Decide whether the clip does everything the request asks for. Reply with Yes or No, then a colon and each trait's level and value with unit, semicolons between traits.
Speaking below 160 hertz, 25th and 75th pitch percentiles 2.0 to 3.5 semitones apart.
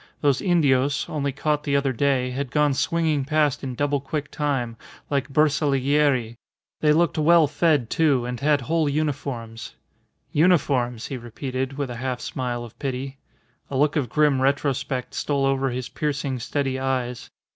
Yes: medium, 140 Hz; narrow, 2.6 semitones